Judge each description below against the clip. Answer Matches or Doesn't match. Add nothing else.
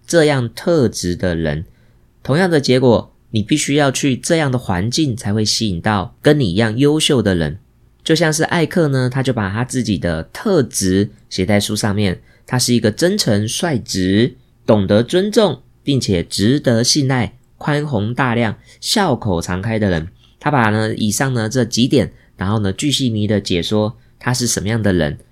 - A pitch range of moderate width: Matches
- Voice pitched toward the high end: Doesn't match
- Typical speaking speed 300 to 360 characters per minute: Doesn't match